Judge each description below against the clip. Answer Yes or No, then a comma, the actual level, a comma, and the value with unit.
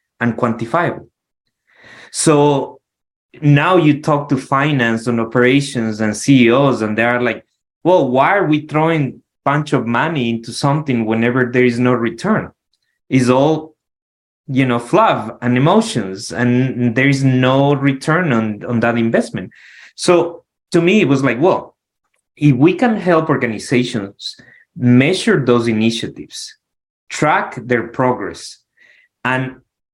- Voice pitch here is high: No, low, 125 Hz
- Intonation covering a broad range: No, average, 3.4 semitones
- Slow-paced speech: Yes, slow, 130 wpm